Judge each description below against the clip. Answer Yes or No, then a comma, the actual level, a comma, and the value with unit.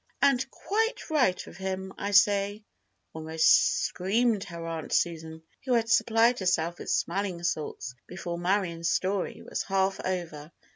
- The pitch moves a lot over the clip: No, average, 3.8 semitones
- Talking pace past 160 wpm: No, average, 140 wpm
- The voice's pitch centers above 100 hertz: Yes, high, 190 Hz